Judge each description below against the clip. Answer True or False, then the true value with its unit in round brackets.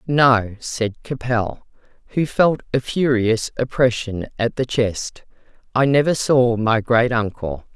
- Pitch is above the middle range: False (120 Hz)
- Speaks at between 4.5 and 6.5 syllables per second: False (3.7 syllables/s)